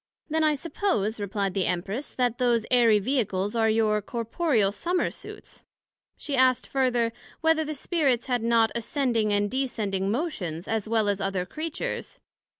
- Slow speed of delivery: No, average, 155 wpm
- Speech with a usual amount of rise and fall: Yes, average, 4.8 semitones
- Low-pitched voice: No, high, 230 Hz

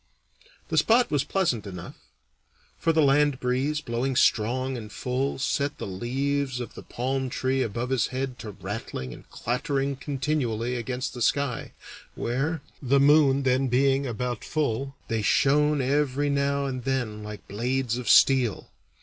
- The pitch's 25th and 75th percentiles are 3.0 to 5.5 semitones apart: No, narrow, 2.6 semitones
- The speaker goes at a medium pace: Yes, average, 150 wpm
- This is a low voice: Yes, low, 130 Hz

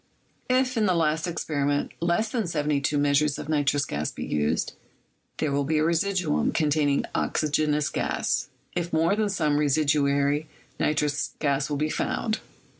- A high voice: No, medium, 150 Hz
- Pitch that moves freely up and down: No, average, 2.8 semitones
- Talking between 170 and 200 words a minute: No, average, 150 wpm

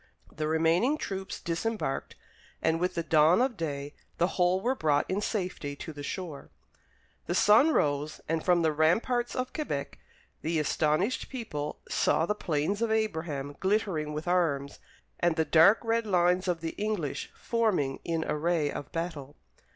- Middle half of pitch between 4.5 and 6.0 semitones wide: Yes, average, 5.2 semitones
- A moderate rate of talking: Yes, average, 160 wpm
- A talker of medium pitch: Yes, medium, 170 Hz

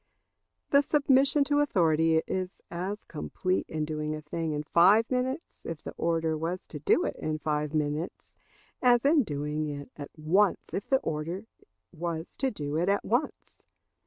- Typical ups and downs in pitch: No, wide, 6.4 semitones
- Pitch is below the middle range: No, medium, 165 Hz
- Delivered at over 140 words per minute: Yes, average, 165 wpm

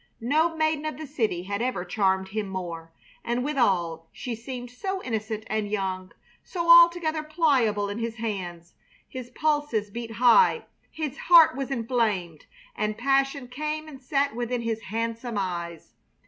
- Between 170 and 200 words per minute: No, average, 150 wpm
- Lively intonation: Yes, wide, 6.2 semitones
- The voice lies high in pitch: Yes, high, 235 Hz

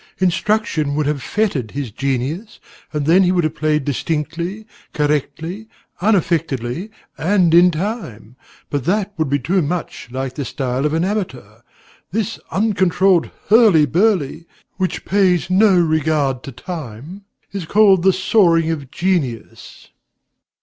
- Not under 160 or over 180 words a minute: No, slow, 135 wpm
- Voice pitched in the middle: Yes, medium, 165 Hz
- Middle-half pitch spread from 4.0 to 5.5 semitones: Yes, average, 5.0 semitones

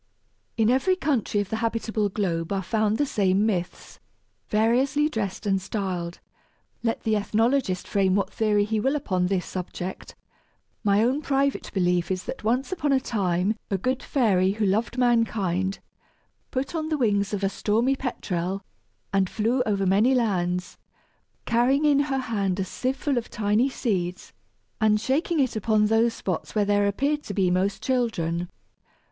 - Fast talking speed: No, average, 165 wpm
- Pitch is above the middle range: Yes, high, 215 Hz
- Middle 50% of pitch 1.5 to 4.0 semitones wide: No, average, 4.7 semitones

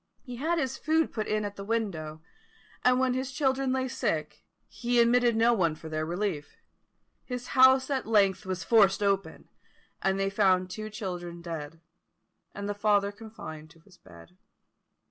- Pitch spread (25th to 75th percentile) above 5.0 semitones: Yes, wide, 5.6 semitones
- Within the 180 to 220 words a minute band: No, average, 165 wpm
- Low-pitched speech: No, high, 205 Hz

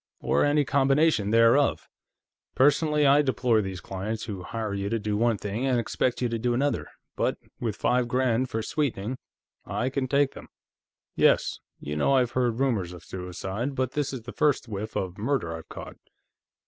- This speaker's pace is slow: No, average, 180 wpm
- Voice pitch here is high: No, low, 120 Hz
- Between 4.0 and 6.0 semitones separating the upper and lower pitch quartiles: Yes, average, 4.5 semitones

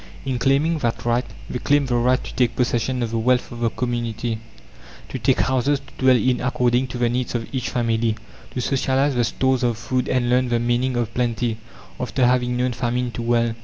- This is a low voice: Yes, low, 125 Hz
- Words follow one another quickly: Yes, fast, 210 wpm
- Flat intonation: Yes, narrow, 1.3 semitones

